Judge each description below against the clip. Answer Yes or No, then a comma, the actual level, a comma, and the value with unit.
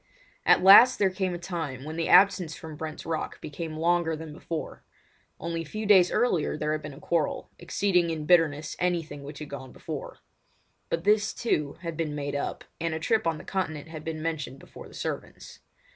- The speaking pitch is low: No, medium, 160 Hz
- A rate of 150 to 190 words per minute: No, average, 200 wpm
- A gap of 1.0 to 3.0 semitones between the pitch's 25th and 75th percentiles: Yes, average, 2.7 semitones